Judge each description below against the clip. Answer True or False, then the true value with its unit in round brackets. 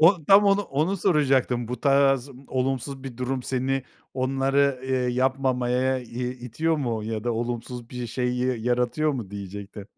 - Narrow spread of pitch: True (2.1 semitones)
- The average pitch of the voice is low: True (130 Hz)